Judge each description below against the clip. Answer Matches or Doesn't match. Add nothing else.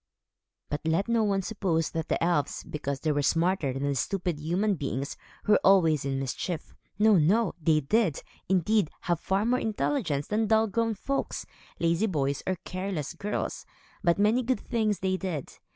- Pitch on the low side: Doesn't match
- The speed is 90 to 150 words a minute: Doesn't match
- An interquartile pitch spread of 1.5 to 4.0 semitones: Doesn't match